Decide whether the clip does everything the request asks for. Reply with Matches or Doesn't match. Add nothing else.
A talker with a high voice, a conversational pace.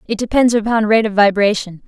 Matches